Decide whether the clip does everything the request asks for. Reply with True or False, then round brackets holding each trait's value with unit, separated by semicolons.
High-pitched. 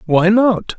True (200 Hz)